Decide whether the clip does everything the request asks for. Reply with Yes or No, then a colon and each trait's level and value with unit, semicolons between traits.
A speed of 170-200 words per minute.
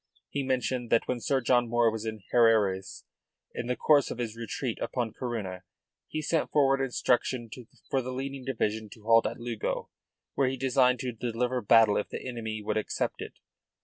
Yes: average, 180 wpm